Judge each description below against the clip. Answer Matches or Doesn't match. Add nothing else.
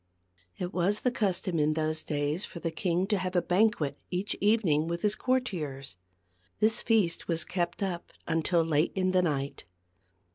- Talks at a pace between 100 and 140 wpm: Doesn't match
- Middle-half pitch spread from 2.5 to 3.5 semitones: Doesn't match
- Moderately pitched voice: Matches